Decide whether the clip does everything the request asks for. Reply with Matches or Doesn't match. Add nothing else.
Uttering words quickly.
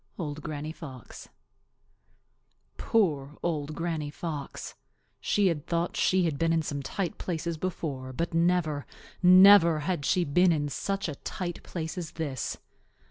Doesn't match